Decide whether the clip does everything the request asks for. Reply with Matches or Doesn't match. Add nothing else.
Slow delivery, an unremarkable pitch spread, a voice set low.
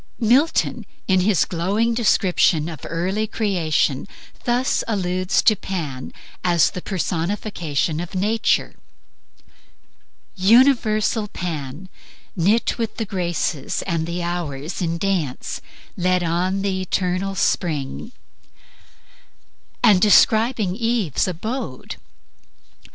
Doesn't match